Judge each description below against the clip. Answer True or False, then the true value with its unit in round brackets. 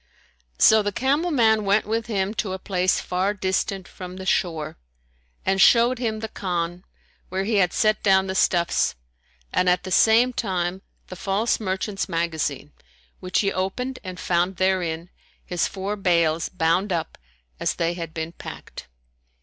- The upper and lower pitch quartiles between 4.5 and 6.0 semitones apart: False (3.2 semitones)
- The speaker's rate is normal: True (160 wpm)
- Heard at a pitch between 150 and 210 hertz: True (190 Hz)